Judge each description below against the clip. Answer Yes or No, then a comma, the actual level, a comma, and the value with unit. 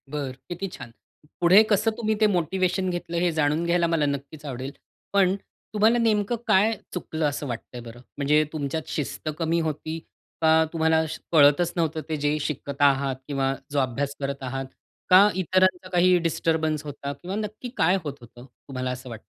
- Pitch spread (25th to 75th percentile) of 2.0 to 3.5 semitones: No, average, 4.3 semitones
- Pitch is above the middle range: No, medium, 160 Hz